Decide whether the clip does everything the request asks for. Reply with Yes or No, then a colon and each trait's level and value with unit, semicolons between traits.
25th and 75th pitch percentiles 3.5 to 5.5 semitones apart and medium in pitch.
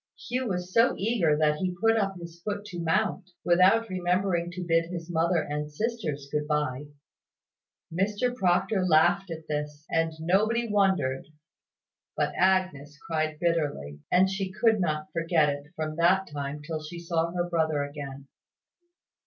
Yes: average, 3.9 semitones; medium, 170 Hz